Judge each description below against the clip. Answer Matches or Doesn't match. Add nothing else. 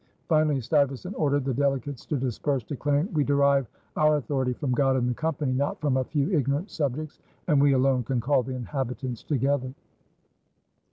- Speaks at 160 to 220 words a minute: Matches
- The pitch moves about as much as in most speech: Doesn't match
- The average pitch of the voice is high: Doesn't match